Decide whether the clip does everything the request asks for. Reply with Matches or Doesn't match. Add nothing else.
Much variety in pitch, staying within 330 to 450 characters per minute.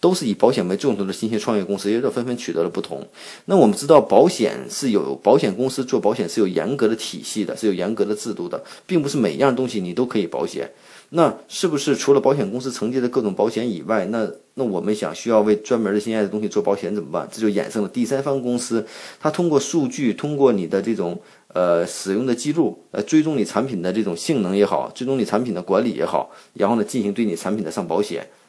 Doesn't match